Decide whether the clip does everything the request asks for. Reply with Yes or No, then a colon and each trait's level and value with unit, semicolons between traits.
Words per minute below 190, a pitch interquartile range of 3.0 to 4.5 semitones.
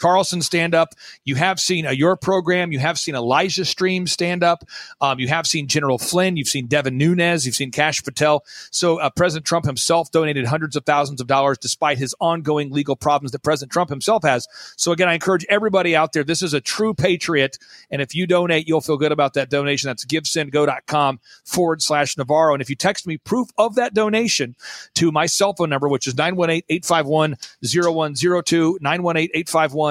No: average, 195 wpm; average, 3.4 semitones